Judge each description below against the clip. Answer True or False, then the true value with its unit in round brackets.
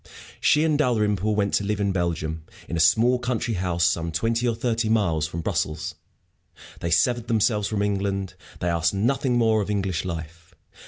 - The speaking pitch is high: False (100 Hz)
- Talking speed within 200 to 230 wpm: False (175 wpm)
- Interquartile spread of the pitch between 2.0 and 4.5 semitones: False (5.1 semitones)